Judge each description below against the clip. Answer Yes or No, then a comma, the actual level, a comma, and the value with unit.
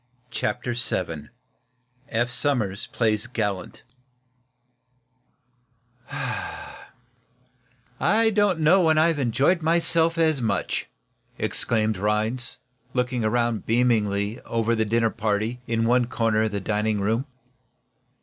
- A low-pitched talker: Yes, low, 120 Hz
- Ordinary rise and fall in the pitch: Yes, average, 3.0 semitones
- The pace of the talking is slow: Yes, slow, 100 wpm